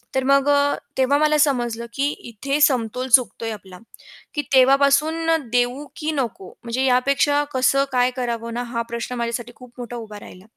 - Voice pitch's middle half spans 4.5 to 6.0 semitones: No, average, 2.9 semitones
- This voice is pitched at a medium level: No, very high, 255 Hz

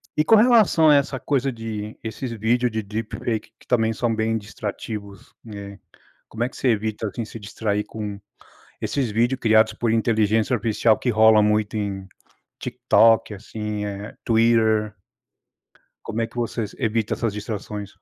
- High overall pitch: No, low, 110 Hz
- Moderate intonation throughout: No, narrow, 1.7 semitones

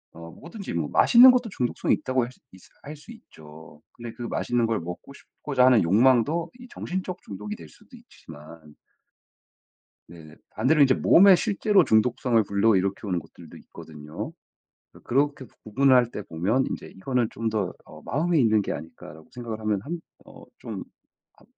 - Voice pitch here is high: No, low, 115 Hz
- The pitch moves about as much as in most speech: No, wide, 7.4 semitones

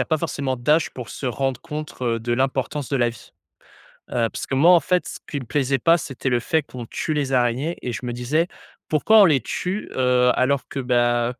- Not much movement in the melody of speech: No, average, 3.6 semitones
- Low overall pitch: Yes, low, 130 Hz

